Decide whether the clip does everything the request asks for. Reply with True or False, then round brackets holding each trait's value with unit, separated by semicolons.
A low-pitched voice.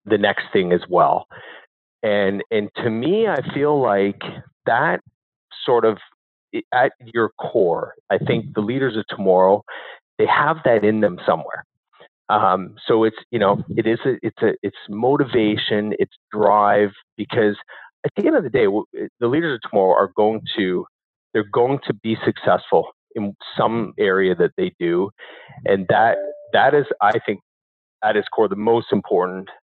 True (110 Hz)